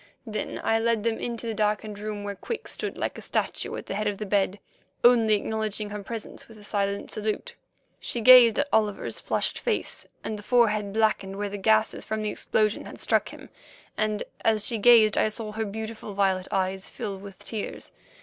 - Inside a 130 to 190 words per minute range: No, average, 200 wpm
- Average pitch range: No, narrow, 1.5 semitones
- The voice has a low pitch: No, high, 215 Hz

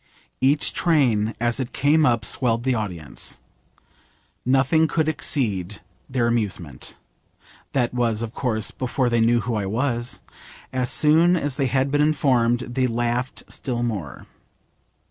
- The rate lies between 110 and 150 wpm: Yes, average, 140 wpm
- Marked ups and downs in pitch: No, average, 3.0 semitones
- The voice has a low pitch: Yes, low, 120 Hz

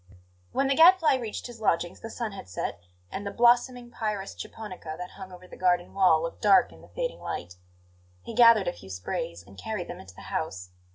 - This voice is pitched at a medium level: No, high, 200 Hz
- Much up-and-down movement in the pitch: Yes, wide, 6.1 semitones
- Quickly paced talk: Yes, fast, 210 wpm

